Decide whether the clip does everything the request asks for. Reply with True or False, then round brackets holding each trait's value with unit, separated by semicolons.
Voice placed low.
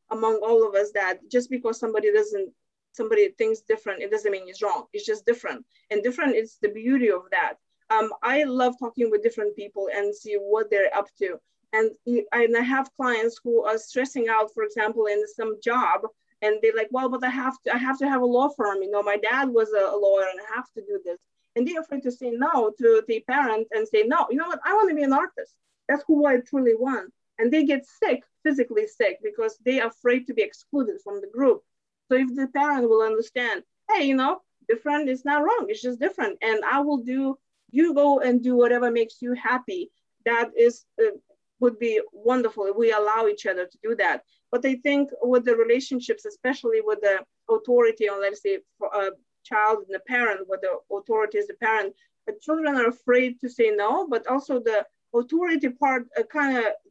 False (250 Hz)